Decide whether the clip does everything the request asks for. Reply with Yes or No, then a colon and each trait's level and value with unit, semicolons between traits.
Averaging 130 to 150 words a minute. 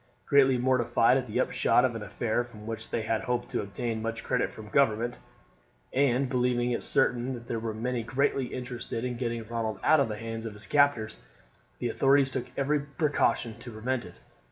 No: average, 195 wpm